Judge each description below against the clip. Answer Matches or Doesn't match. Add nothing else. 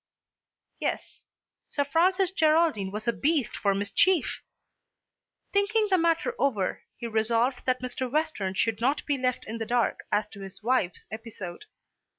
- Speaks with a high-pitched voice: Matches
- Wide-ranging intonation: Matches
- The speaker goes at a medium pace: Matches